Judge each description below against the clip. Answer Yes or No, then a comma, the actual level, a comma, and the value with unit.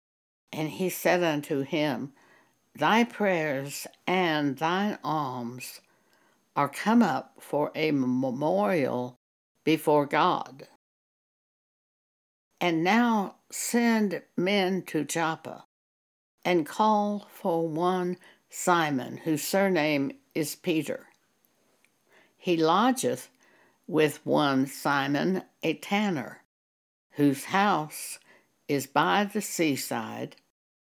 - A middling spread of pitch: Yes, average, 4.8 semitones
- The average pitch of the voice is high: No, medium, 160 Hz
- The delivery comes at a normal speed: No, slow, 90 wpm